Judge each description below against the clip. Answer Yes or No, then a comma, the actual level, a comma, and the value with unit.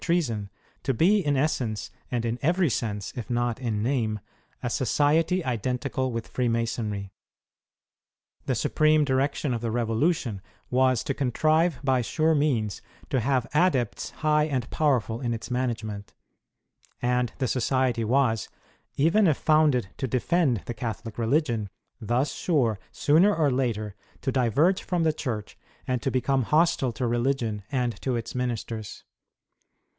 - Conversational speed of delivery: Yes, average, 145 wpm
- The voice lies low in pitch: Yes, low, 125 Hz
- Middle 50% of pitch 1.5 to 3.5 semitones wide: No, average, 4.2 semitones